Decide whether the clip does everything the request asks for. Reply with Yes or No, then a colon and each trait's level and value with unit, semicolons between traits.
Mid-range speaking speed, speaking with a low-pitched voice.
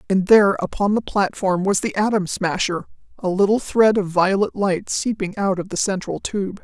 No: average, 190 wpm; high, 195 Hz